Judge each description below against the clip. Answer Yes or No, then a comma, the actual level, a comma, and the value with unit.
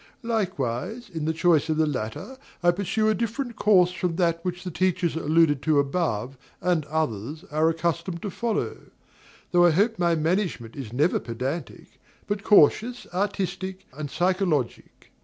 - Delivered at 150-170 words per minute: Yes, average, 155 wpm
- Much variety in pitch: No, average, 3.9 semitones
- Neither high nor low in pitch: Yes, medium, 170 Hz